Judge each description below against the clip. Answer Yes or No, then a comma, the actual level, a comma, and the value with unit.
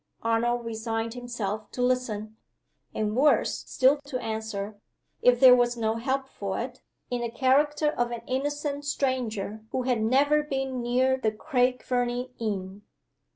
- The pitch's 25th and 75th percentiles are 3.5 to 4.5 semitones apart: No, average, 2.9 semitones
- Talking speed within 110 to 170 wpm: Yes, average, 150 wpm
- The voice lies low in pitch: No, high, 245 Hz